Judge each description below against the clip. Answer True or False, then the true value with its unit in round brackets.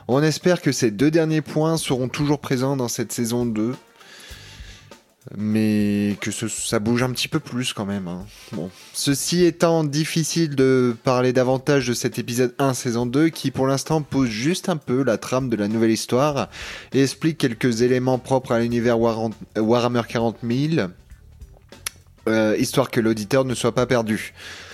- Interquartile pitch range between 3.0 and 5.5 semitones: True (3.6 semitones)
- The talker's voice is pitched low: True (125 Hz)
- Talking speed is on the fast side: False (170 wpm)